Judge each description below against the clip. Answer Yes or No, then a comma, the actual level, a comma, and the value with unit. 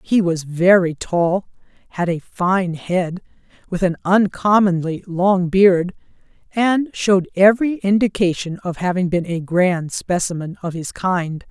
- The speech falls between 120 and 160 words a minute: Yes, slow, 135 wpm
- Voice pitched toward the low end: No, medium, 185 Hz